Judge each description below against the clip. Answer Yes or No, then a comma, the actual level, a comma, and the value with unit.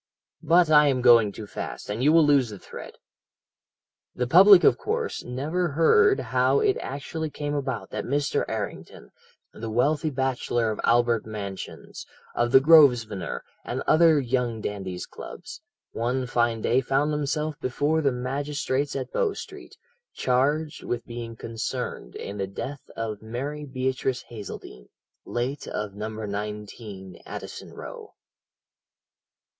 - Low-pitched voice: Yes, low, 130 Hz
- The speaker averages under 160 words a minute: Yes, average, 140 wpm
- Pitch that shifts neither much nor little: Yes, average, 4.7 semitones